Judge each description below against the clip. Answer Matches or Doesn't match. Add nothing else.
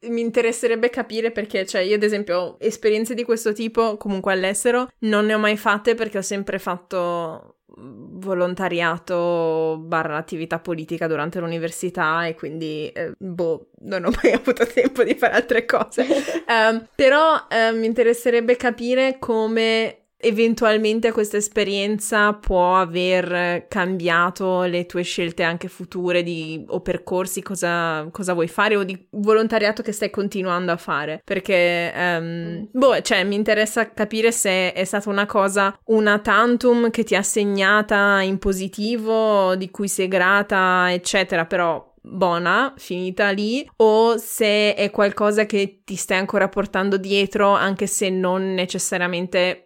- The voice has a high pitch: Matches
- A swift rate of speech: Doesn't match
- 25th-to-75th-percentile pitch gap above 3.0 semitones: Matches